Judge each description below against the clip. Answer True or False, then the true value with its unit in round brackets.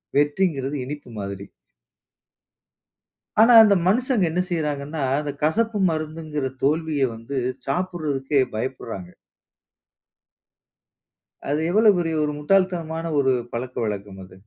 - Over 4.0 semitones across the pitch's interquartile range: True (4.7 semitones)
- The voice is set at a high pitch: False (150 Hz)